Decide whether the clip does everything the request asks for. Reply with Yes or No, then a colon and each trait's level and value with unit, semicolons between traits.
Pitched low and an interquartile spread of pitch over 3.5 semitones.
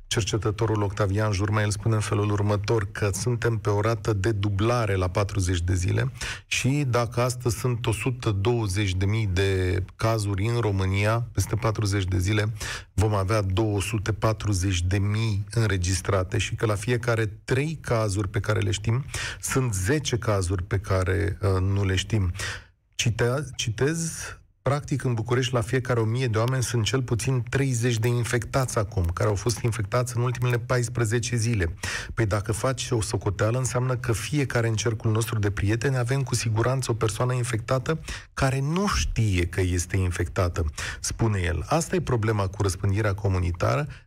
No: low, 110 Hz; average, 3.2 semitones